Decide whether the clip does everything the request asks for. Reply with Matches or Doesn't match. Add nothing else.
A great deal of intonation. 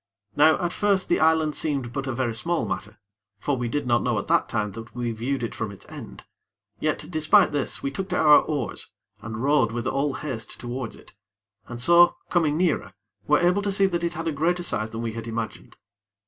Matches